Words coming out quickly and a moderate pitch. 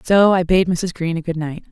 Yes: fast, 280 wpm; medium, 175 Hz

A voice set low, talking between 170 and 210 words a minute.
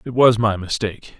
Yes: low, 110 Hz; average, 200 wpm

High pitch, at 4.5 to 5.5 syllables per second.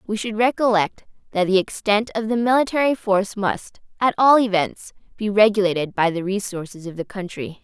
Yes: high, 205 Hz; 5.4 syllables/s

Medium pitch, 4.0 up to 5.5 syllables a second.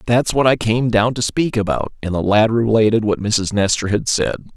No: low, 110 Hz; 5.1 syllables/s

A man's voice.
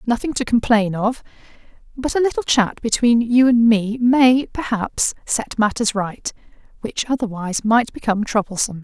No: female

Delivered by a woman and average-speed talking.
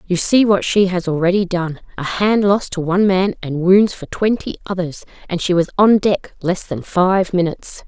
Yes: female; average, 190 wpm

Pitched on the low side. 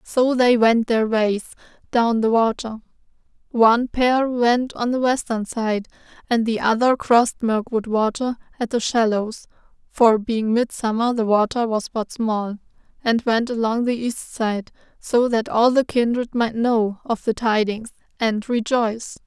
No: high, 230 Hz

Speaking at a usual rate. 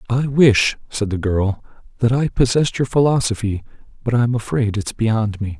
Yes: average, 195 wpm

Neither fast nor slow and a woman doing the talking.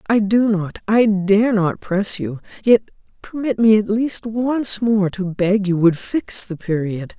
Yes: average, 175 wpm; female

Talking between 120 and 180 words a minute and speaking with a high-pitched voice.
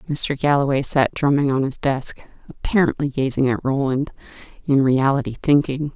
No: average, 140 wpm; medium, 140 Hz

